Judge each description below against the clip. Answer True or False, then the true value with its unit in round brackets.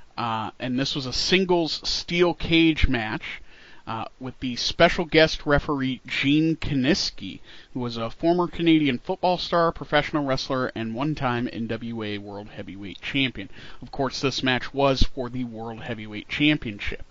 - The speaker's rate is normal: True (150 wpm)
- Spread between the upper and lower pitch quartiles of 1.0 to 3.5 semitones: False (5.2 semitones)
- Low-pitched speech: True (130 Hz)